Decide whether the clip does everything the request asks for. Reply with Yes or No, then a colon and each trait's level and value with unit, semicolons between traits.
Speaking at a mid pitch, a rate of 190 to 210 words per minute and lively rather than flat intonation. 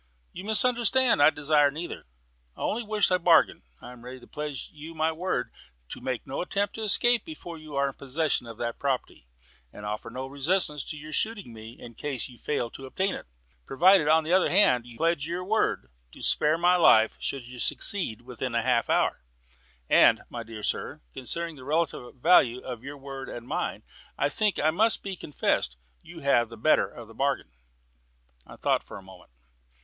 Yes: medium, 145 Hz; average, 200 wpm; wide, 6.1 semitones